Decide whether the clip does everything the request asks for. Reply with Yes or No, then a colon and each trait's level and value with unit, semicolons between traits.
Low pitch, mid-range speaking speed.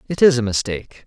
No: low, 115 Hz; fast, 225 wpm